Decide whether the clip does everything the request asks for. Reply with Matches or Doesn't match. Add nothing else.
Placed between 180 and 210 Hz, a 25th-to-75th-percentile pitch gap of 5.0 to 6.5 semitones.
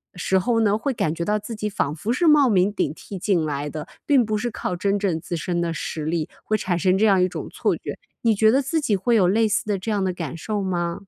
Doesn't match